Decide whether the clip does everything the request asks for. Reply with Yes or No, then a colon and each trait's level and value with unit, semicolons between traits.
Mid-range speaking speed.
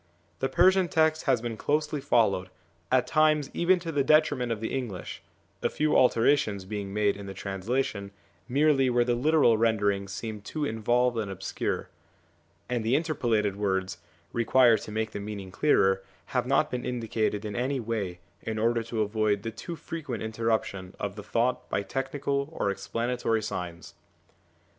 Yes: average, 160 wpm